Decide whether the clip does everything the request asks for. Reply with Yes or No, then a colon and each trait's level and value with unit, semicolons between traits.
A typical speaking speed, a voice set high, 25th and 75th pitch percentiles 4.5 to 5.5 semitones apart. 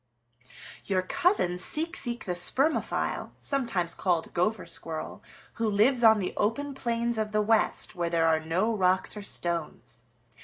Yes: average, 150 wpm; high, 205 Hz; average, 5.1 semitones